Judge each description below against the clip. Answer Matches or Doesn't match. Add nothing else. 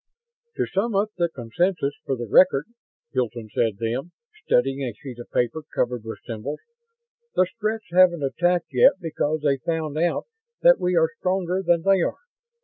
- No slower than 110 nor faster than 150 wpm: Doesn't match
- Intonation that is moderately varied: Doesn't match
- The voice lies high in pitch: Doesn't match